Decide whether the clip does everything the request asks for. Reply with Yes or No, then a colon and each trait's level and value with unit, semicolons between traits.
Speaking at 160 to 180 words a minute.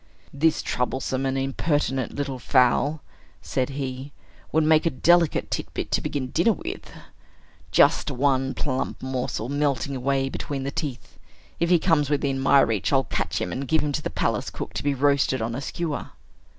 Yes: average, 175 wpm